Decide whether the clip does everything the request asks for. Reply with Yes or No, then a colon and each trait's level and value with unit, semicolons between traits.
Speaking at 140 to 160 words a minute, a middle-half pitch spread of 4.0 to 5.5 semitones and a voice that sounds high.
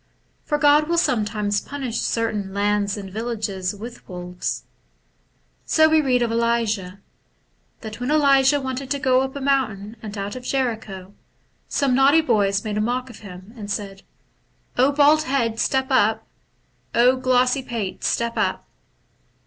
Yes: average, 150 wpm; average, 4.5 semitones; high, 235 Hz